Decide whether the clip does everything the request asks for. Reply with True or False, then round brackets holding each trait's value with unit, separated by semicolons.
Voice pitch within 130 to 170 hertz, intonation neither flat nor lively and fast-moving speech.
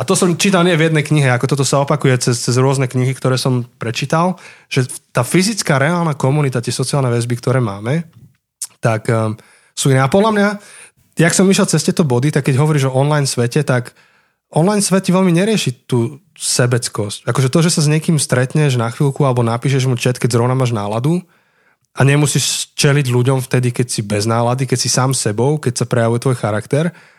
True (135 Hz; 4.1 semitones; 200 wpm)